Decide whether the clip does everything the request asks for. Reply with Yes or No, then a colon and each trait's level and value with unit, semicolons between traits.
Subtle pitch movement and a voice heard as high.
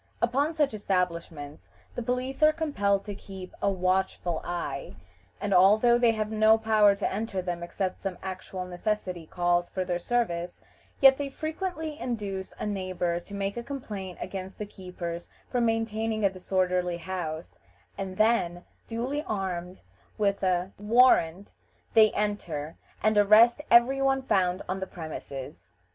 No: average, 4.0 semitones; high, 195 Hz